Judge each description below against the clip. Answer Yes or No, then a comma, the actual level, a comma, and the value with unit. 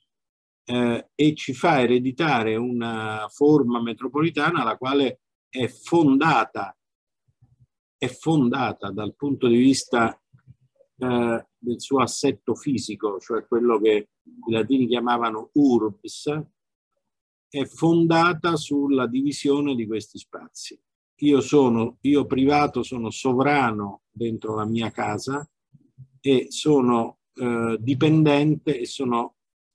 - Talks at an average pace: No, slow, 105 wpm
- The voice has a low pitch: Yes, low, 130 Hz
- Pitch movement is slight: No, average, 3.7 semitones